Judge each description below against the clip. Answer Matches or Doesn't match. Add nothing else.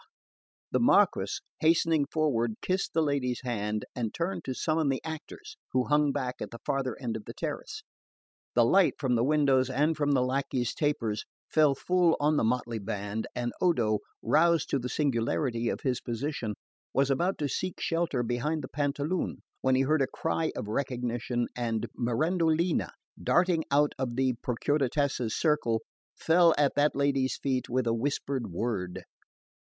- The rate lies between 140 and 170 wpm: Matches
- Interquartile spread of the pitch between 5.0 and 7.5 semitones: Doesn't match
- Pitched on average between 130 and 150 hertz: Matches